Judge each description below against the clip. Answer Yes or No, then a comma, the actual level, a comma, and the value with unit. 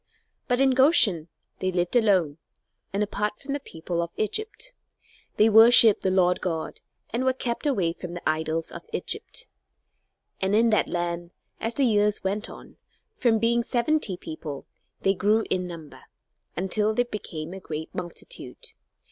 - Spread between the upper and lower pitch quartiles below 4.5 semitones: No, wide, 5.4 semitones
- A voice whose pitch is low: No, high, 205 Hz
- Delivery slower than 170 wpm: Yes, average, 155 wpm